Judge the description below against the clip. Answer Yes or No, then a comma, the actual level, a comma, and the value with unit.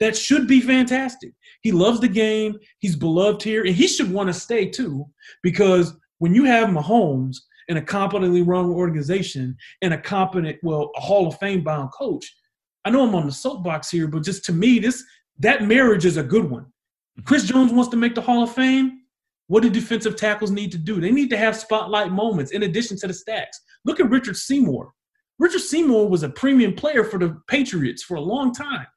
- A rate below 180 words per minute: No, fast, 205 wpm